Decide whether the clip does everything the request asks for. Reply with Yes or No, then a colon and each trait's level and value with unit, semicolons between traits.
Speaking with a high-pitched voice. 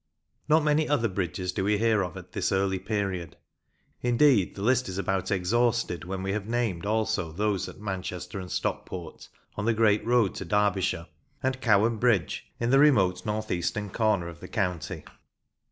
No: low, 100 Hz